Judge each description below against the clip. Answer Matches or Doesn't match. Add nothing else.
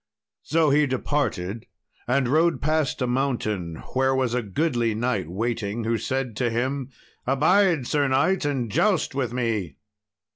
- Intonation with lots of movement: Doesn't match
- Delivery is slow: Doesn't match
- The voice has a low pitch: Matches